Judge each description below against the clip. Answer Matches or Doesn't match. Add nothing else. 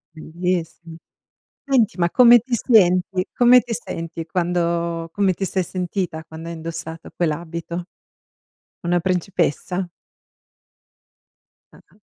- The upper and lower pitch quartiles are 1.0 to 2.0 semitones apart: Doesn't match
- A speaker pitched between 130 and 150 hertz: Doesn't match